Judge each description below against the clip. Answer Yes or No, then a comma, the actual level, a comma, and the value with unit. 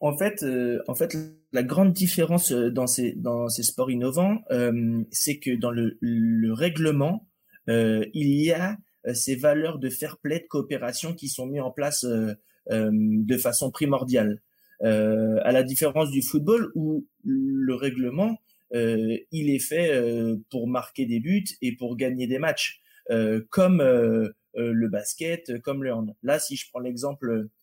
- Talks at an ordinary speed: Yes, average, 170 wpm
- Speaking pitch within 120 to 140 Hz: Yes, low, 130 Hz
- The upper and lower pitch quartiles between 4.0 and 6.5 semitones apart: Yes, average, 5.0 semitones